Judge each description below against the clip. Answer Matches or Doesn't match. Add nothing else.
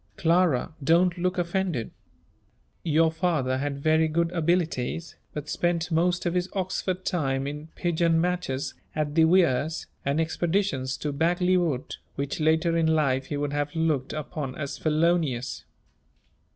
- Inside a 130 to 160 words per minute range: Matches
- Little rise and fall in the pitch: Doesn't match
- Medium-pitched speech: Matches